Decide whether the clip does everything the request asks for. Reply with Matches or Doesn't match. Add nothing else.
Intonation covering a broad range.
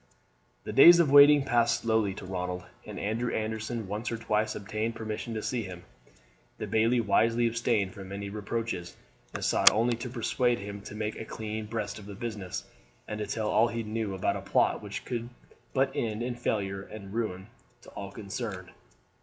Doesn't match